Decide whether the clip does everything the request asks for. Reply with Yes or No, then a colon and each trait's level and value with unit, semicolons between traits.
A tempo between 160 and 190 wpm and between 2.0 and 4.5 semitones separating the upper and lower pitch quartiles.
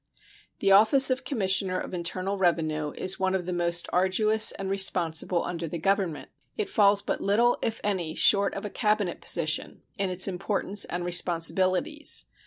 Yes: average, 165 wpm; average, 2.9 semitones